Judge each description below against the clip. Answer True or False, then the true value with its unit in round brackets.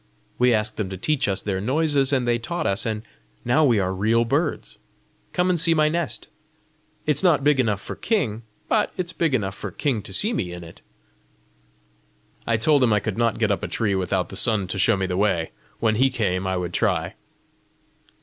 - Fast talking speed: True (210 wpm)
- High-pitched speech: False (115 Hz)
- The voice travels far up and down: True (6.6 semitones)